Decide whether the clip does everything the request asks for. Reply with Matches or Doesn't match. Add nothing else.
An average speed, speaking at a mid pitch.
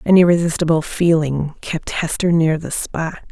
Matches